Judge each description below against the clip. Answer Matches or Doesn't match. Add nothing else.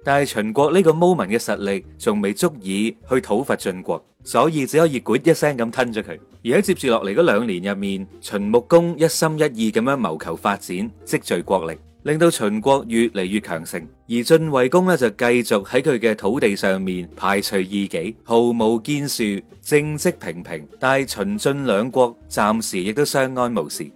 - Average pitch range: Doesn't match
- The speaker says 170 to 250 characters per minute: Doesn't match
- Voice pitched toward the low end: Matches